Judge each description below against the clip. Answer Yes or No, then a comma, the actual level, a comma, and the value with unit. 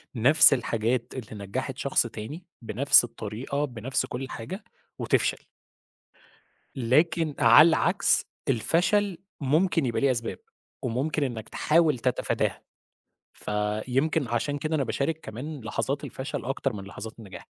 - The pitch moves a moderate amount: Yes, average, 4.8 semitones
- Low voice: Yes, low, 130 Hz